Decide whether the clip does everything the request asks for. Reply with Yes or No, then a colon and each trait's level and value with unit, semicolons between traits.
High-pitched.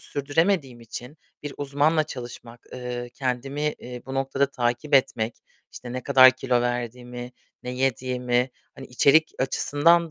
No: low, 130 Hz